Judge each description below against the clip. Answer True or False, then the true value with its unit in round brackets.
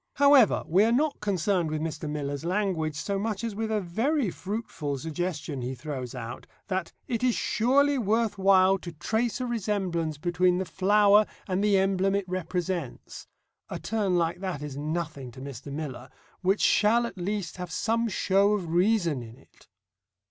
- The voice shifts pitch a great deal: False (4.9 semitones)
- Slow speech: False (170 wpm)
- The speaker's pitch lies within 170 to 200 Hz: True (185 Hz)